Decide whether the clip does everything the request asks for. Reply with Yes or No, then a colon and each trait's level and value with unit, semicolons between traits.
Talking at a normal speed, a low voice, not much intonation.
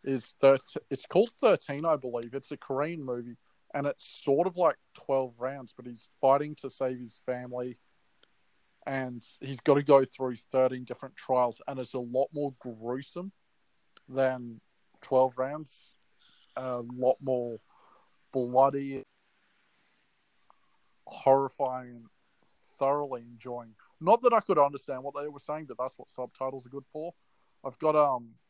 Yes: average, 145 wpm; low, 130 Hz; narrow, 2.1 semitones